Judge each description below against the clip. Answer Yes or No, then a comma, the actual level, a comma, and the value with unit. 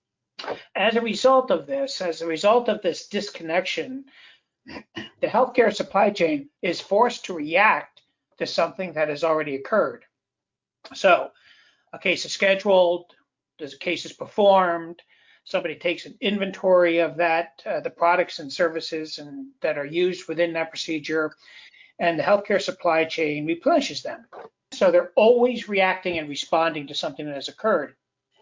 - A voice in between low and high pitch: Yes, medium, 175 Hz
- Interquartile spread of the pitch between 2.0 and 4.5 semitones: Yes, average, 4.1 semitones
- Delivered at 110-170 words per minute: Yes, average, 150 wpm